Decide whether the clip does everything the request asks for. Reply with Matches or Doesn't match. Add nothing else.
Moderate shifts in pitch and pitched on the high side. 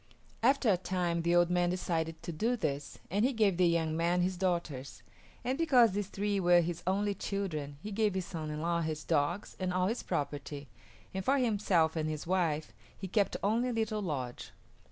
Doesn't match